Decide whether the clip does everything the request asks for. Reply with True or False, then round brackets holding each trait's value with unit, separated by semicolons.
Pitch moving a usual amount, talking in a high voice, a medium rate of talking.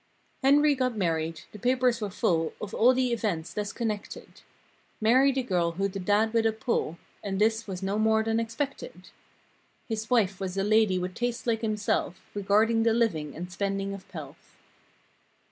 True (3.3 semitones; 215 Hz; 185 wpm)